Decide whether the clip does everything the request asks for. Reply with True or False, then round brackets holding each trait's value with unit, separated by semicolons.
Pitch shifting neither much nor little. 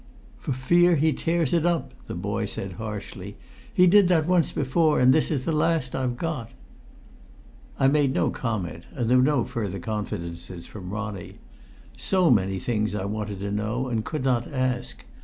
False (6.7 semitones)